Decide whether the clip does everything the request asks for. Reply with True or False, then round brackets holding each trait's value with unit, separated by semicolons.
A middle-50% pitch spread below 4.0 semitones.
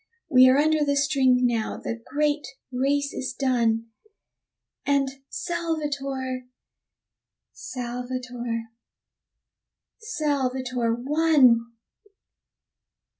True (2.7 semitones)